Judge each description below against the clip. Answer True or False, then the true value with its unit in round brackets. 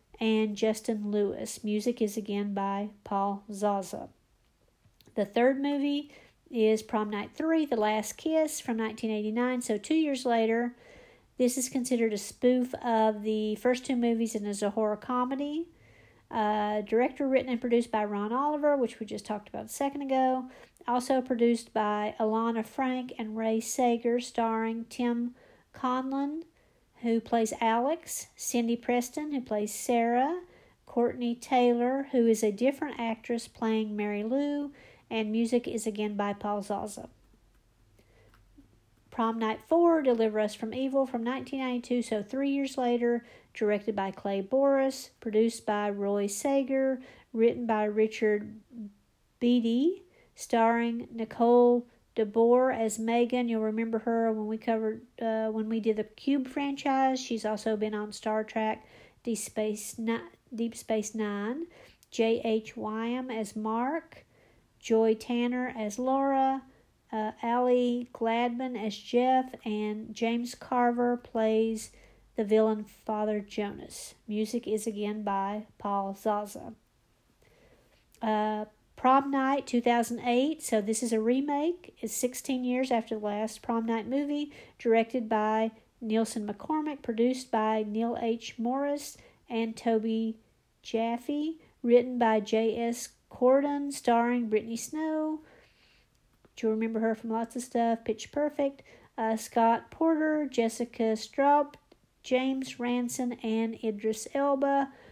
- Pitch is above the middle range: True (230 Hz)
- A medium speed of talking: False (130 wpm)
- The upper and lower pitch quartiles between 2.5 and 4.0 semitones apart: True (2.8 semitones)